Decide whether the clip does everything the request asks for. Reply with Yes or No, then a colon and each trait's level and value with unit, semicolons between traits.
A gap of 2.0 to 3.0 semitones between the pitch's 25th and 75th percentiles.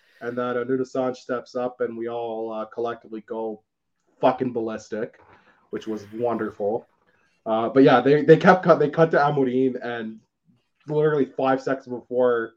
Yes: average, 2.7 semitones